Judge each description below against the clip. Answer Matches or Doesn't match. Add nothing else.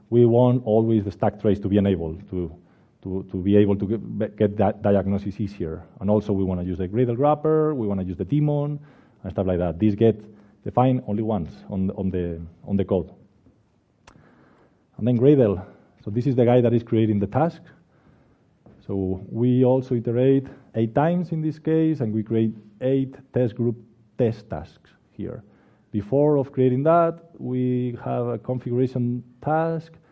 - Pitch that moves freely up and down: Doesn't match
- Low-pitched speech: Matches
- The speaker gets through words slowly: Doesn't match